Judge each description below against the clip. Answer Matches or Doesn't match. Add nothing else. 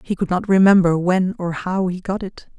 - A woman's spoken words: Matches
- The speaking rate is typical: Doesn't match